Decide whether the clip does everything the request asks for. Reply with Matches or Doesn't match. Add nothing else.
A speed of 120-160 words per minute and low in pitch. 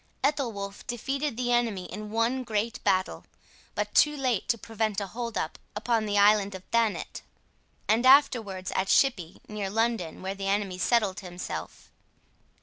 Doesn't match